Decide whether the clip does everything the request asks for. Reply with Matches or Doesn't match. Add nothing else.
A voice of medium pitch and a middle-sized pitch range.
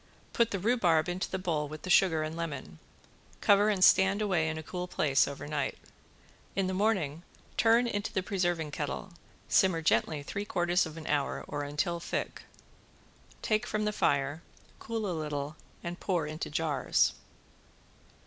Matches